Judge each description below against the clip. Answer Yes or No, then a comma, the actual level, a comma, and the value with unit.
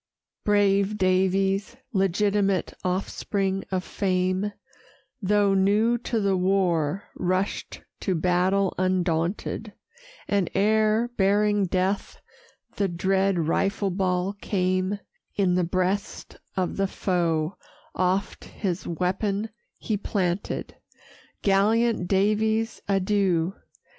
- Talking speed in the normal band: No, slow, 95 wpm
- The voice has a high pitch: Yes, high, 195 Hz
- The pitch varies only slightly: Yes, narrow, 1.9 semitones